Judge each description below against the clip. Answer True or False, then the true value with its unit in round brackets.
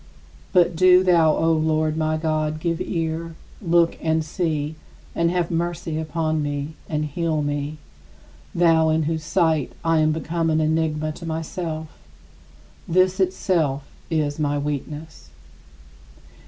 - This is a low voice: False (160 Hz)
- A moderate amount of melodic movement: False (1.5 semitones)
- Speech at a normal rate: False (130 wpm)